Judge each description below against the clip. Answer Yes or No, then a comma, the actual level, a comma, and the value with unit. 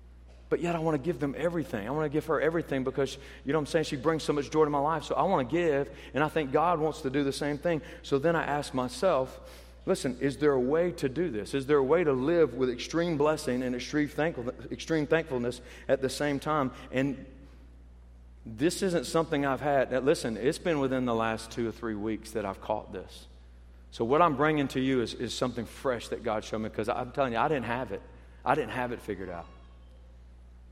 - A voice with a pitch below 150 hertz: Yes, low, 135 Hz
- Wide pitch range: Yes, wide, 6.0 semitones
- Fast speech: Yes, fast, 240 wpm